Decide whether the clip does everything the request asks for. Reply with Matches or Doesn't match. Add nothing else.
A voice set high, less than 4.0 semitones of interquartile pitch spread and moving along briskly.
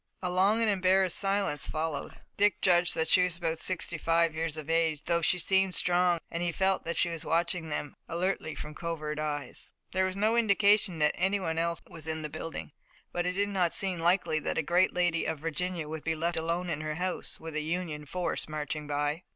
Doesn't match